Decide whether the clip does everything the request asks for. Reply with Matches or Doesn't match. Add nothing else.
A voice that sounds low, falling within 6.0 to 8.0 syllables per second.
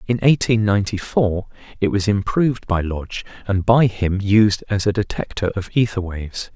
Doesn't match